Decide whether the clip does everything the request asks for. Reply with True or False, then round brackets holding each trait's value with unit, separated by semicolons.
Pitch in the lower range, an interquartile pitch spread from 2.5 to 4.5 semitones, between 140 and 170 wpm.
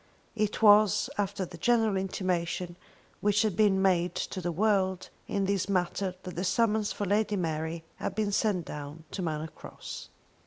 False (190 Hz; 2.9 semitones; 165 wpm)